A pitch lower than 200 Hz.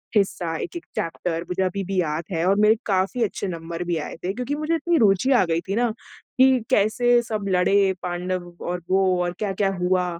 Yes: high, 190 Hz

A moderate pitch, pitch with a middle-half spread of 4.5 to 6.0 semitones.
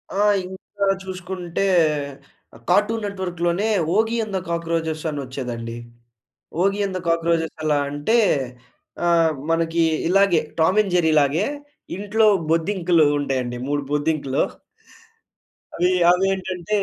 No: medium, 170 Hz; average, 3.4 semitones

